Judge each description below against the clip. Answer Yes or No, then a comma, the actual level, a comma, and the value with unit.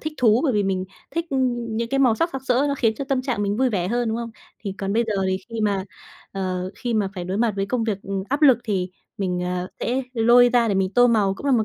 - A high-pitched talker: Yes, high, 225 Hz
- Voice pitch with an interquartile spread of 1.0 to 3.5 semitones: No, average, 4.0 semitones